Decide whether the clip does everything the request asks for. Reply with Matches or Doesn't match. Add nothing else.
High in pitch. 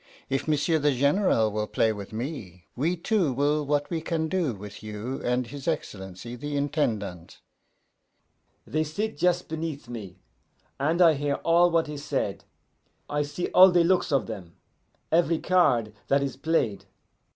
Doesn't match